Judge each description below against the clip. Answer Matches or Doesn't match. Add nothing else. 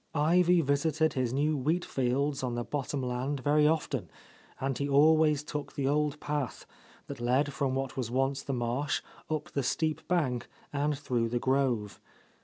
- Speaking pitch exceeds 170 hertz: Doesn't match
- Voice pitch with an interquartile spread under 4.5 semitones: Matches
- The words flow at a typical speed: Matches